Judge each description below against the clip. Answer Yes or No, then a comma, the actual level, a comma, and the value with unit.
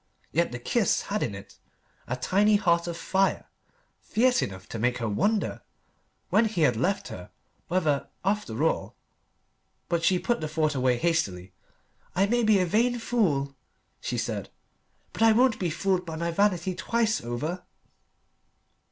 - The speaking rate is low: No, average, 160 wpm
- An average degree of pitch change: No, wide, 7.2 semitones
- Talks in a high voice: No, medium, 175 Hz